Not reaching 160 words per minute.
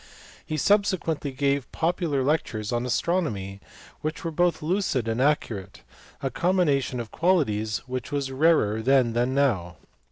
Yes: slow, 135 wpm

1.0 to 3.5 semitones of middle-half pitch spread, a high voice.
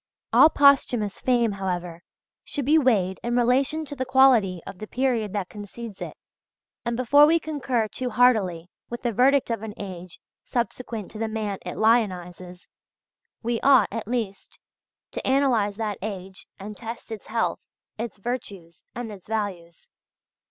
No: average, 4.1 semitones; high, 225 Hz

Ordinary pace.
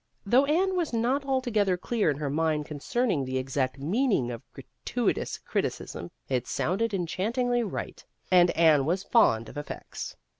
Yes: average, 150 wpm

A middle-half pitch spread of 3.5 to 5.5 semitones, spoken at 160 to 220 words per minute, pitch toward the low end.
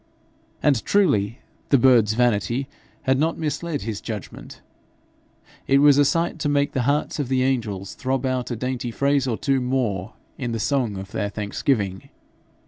Yes: average, 4.1 semitones; average, 165 wpm; low, 130 Hz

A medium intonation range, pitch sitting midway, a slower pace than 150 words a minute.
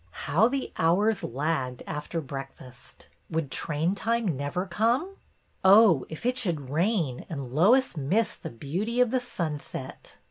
No: wide, 7.7 semitones; medium, 170 Hz; average, 140 wpm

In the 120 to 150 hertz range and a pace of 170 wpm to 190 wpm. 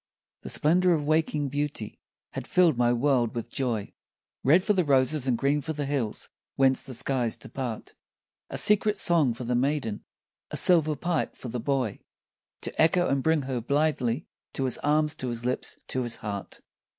Yes: low, 135 Hz; average, 180 wpm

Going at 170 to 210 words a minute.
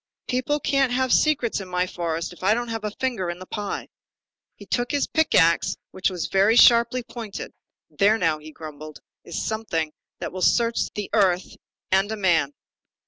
Yes: average, 185 wpm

